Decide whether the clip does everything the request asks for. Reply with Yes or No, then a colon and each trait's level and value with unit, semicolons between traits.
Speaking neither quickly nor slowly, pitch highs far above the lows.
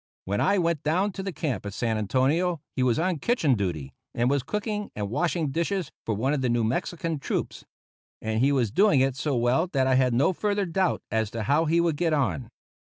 No: fast, 220 wpm; wide, 6.5 semitones